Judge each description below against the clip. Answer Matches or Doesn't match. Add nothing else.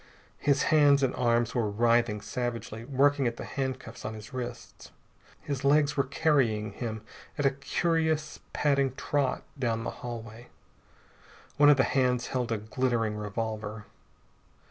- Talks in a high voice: Doesn't match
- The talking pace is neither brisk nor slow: Matches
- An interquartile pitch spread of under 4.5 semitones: Matches